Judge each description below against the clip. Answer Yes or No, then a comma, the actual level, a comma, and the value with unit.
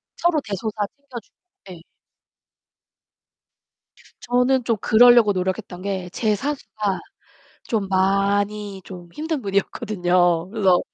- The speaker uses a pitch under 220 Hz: Yes, high, 205 Hz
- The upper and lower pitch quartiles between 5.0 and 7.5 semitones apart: No, average, 3.9 semitones